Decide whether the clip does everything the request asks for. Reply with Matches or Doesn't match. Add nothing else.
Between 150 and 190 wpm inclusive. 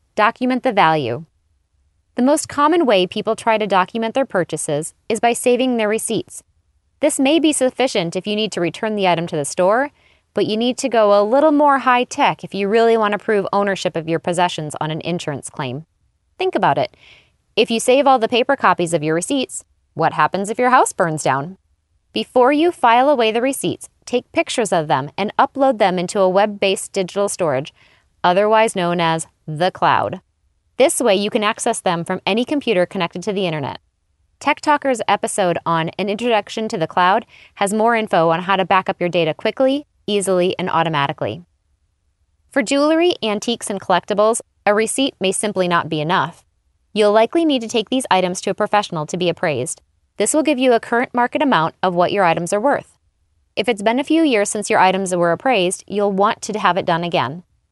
Doesn't match